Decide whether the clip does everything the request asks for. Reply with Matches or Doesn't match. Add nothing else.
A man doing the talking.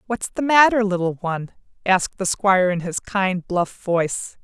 Doesn't match